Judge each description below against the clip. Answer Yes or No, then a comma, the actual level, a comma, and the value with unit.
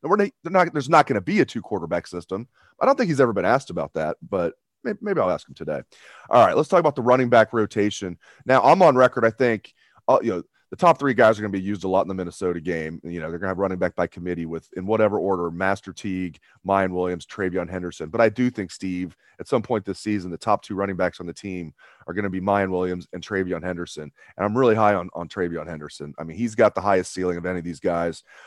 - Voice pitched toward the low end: Yes, very low, 95 Hz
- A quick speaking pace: Yes, fast, 270 wpm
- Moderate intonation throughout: Yes, average, 3.5 semitones